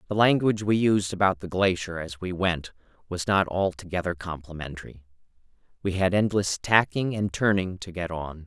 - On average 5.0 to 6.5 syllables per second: Yes, 5.2 syllables/s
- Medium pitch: No, very low, 95 Hz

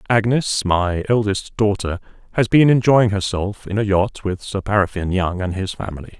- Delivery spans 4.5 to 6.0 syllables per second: Yes, 5.0 syllables/s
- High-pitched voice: No, low, 100 Hz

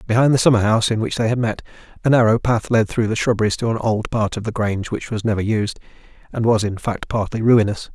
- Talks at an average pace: No, fast, 250 wpm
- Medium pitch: No, low, 110 Hz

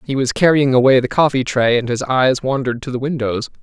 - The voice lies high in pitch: No, low, 130 Hz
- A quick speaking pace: Yes, fast, 230 wpm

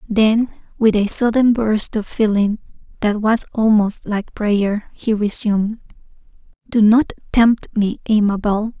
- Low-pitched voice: No, high, 215 Hz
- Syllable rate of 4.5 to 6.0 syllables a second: No, 3.9 syllables/s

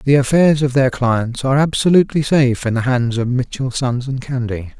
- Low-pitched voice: Yes, low, 130 Hz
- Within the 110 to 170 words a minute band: No, average, 200 wpm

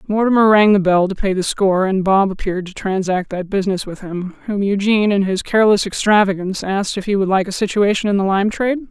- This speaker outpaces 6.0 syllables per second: Yes, 6.3 syllables/s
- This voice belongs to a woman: Yes, female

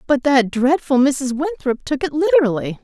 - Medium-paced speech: Yes, average, 170 wpm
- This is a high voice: Yes, very high, 280 Hz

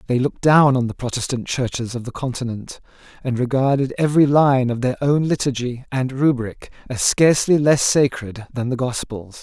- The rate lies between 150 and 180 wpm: Yes, average, 170 wpm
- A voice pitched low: Yes, low, 130 Hz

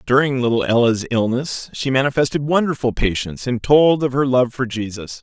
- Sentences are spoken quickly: No, average, 170 wpm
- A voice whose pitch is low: Yes, low, 125 Hz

